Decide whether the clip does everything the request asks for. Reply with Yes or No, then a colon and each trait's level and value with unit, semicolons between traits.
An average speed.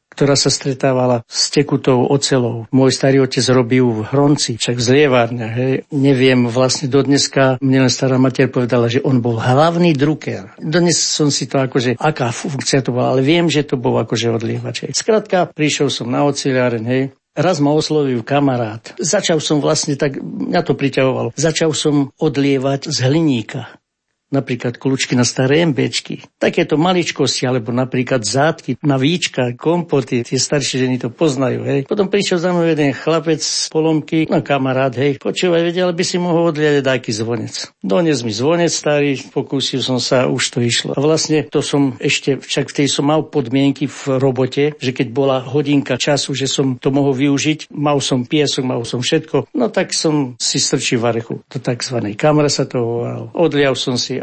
No: fast, 175 wpm